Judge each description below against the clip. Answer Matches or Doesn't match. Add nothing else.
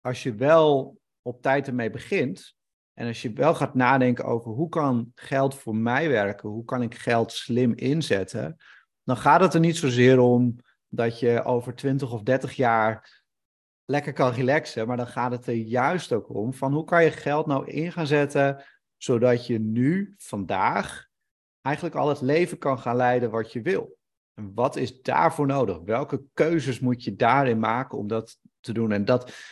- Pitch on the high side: Doesn't match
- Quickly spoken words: Doesn't match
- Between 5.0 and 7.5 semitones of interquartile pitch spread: Doesn't match